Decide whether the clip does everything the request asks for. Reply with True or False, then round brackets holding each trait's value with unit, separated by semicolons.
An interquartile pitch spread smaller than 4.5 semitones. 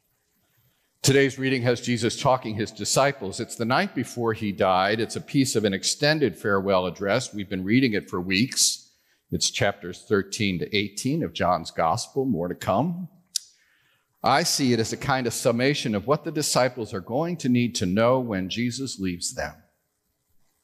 False (5.1 semitones)